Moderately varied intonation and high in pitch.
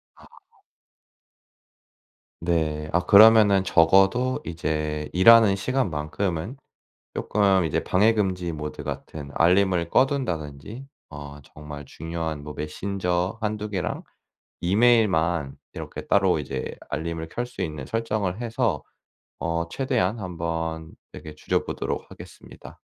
No: average, 5.0 semitones; very low, 90 Hz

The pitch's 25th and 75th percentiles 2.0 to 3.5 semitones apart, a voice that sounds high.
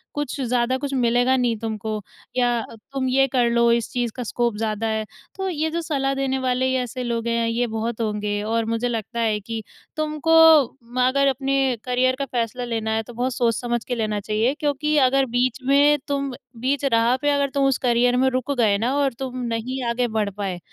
Yes: average, 2.9 semitones; high, 245 Hz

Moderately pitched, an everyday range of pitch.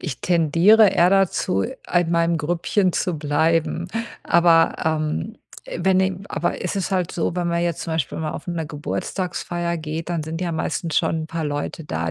No: medium, 165 Hz; narrow, 1.9 semitones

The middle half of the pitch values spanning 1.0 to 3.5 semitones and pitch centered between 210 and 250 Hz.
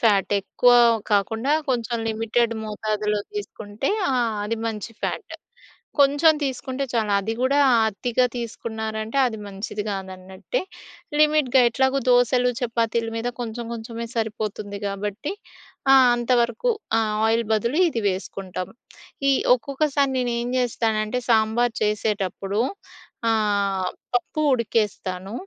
Yes: average, 2.8 semitones; high, 225 Hz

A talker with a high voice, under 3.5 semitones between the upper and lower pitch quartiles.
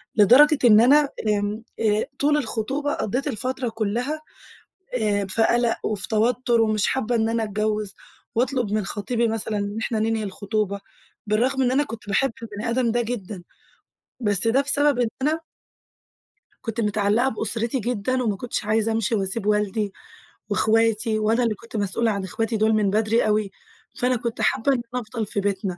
Yes: high, 225 Hz; narrow, 2.6 semitones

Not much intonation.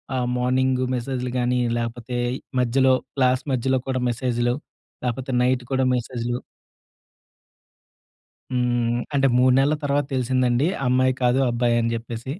Yes: narrow, 1.3 semitones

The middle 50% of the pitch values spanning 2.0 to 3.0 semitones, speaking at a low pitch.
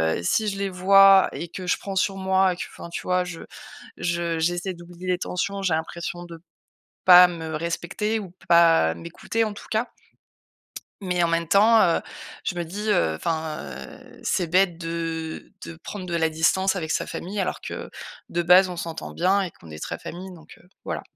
No: narrow, 2.4 semitones; medium, 175 Hz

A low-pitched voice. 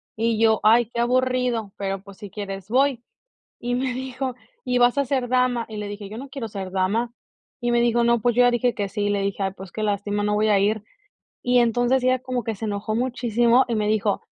No: high, 230 Hz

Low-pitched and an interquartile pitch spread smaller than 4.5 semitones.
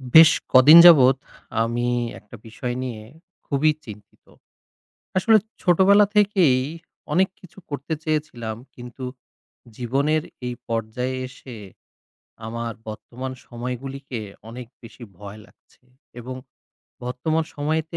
No: low, 130 Hz; average, 4.8 semitones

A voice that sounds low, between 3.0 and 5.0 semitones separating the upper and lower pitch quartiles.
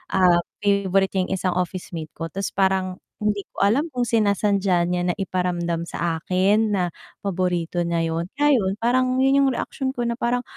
No: high, 190 Hz; average, 4.2 semitones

